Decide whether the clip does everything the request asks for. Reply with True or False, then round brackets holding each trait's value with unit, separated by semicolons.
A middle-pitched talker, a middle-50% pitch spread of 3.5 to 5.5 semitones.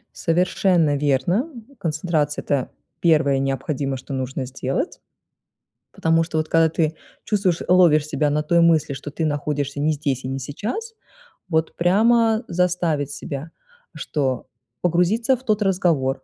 True (155 Hz; 4.0 semitones)